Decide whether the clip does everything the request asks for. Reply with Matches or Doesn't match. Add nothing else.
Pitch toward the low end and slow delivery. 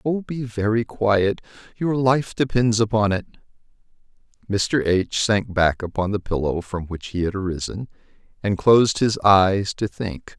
Doesn't match